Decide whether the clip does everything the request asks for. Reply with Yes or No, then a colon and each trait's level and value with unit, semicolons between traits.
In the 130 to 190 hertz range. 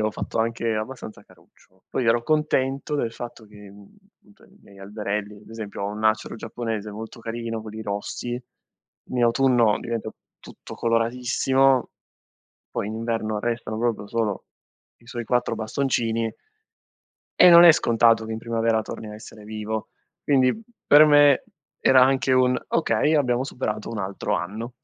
No: low, 115 Hz